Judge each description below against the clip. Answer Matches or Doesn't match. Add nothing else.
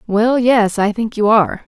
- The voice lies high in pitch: Matches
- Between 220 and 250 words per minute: Doesn't match